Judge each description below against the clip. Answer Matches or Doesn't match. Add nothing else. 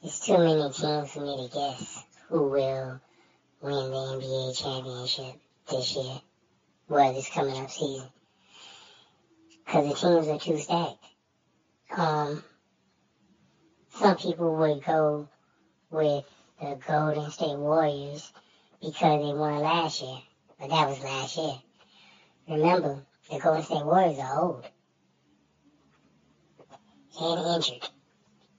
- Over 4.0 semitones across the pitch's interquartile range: Doesn't match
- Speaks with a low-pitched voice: Doesn't match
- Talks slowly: Matches